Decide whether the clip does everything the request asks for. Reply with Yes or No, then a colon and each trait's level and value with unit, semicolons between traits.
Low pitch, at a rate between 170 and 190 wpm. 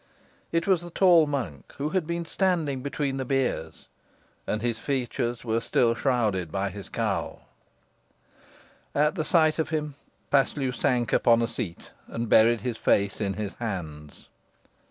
No: low, 125 Hz; average, 150 wpm